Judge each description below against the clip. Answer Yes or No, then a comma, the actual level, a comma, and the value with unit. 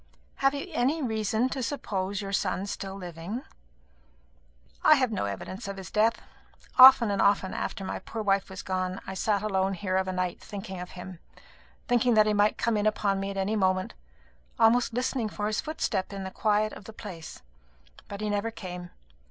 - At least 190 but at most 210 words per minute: Yes, average, 195 wpm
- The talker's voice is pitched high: Yes, high, 205 Hz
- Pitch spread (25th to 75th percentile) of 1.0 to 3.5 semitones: Yes, average, 2.8 semitones